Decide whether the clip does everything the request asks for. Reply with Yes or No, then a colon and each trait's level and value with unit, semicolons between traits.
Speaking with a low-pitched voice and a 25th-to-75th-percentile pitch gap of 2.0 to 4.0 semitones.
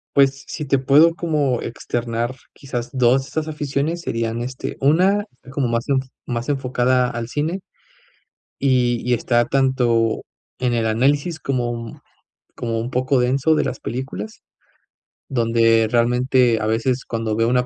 Yes: low, 125 Hz; average, 2.7 semitones